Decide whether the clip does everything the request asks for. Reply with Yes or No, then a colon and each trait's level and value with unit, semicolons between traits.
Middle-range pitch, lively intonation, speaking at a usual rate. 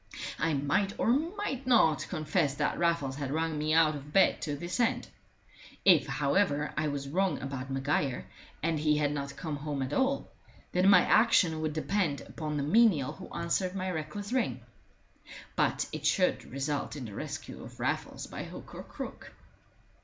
No: medium, 155 Hz; average, 4.6 semitones; average, 175 wpm